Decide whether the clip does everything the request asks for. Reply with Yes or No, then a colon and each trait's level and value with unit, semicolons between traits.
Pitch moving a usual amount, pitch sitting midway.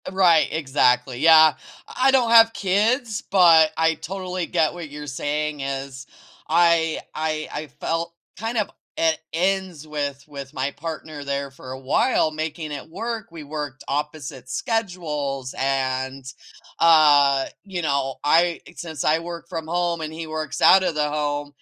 Yes: average, 3.5 semitones; medium, 155 Hz